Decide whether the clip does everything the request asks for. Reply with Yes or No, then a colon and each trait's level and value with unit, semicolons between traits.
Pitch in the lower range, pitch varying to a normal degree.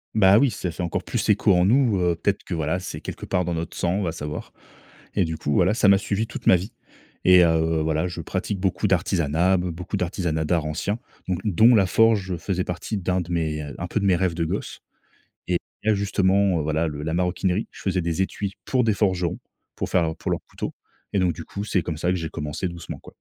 Yes: very low, 90 Hz; average, 3.0 semitones